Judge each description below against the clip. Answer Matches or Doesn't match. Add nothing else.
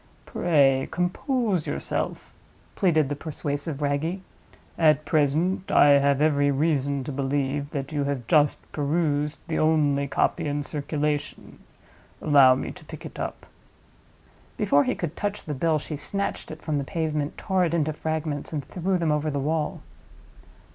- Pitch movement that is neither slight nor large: Doesn't match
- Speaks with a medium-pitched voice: Matches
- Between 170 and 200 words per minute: Doesn't match